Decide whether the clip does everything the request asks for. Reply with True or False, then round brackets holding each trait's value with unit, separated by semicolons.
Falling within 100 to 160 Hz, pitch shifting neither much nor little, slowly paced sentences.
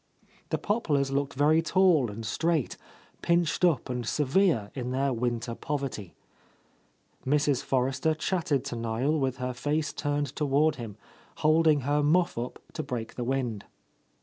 False (140 Hz; 4.0 semitones; 150 wpm)